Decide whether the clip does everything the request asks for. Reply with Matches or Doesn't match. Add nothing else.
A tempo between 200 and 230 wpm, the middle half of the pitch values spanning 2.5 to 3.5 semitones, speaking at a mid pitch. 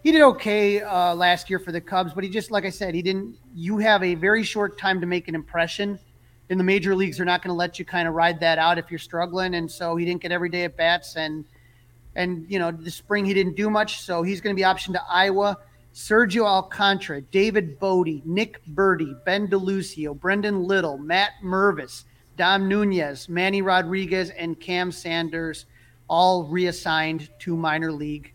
Matches